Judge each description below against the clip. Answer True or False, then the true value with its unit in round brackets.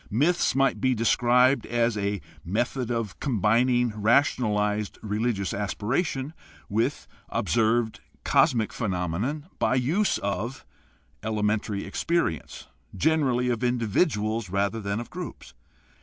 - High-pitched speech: False (115 Hz)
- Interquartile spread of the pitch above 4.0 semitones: False (3.5 semitones)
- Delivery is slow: True (110 wpm)